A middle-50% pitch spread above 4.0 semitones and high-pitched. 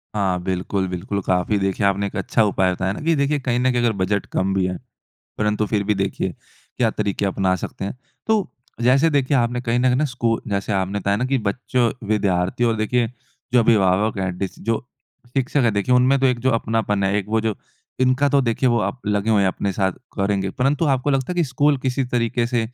No: average, 4.4 semitones; low, 110 Hz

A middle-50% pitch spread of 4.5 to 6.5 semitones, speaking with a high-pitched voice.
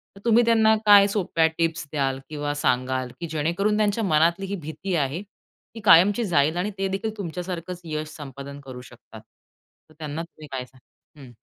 No: average, 5.3 semitones; medium, 165 Hz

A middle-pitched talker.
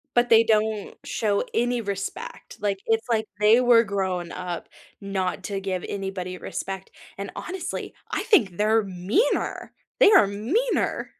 No: high, 205 Hz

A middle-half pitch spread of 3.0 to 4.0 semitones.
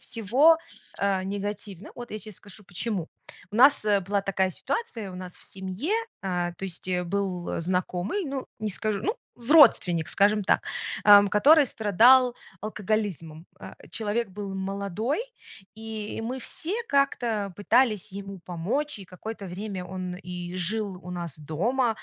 Yes: average, 3.7 semitones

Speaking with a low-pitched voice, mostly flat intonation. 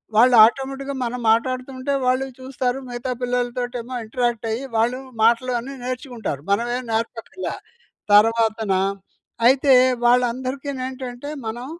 No: very high, 250 Hz; narrow, 1.9 semitones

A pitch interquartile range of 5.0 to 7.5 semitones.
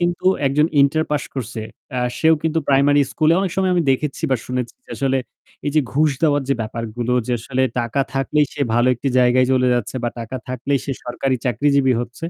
No: average, 3.1 semitones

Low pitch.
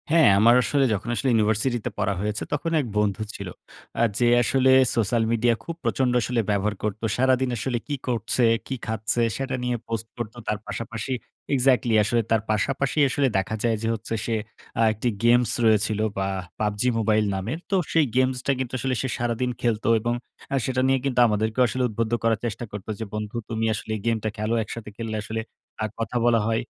Yes: low, 115 Hz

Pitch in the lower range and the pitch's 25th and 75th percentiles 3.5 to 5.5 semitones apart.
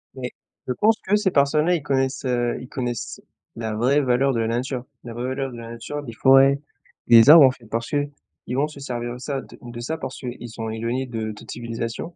No: low, 125 Hz; average, 2.9 semitones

